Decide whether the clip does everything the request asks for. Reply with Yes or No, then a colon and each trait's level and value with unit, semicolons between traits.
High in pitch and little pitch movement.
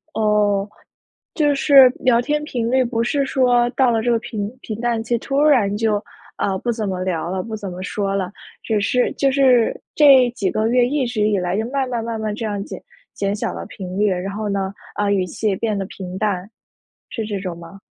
No: high, 220 Hz; average, 3.7 semitones